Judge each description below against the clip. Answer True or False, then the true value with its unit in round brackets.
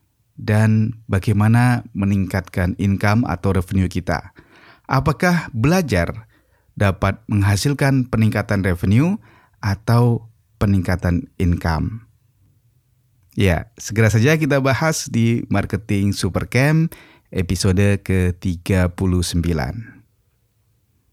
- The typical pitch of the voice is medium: False (105 Hz)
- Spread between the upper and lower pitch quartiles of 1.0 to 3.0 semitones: False (3.5 semitones)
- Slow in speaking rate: True (75 wpm)